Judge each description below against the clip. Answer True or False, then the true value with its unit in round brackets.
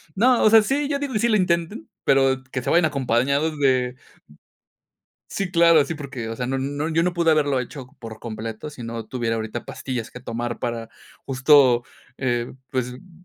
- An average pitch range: False (5.7 semitones)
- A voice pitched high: False (135 Hz)